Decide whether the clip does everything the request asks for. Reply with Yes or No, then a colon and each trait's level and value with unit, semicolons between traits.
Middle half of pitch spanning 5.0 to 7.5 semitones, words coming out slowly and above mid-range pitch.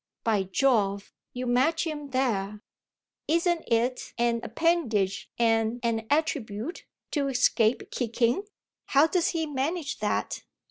Yes: wide, 5.5 semitones; slow, 120 wpm; very high, 250 Hz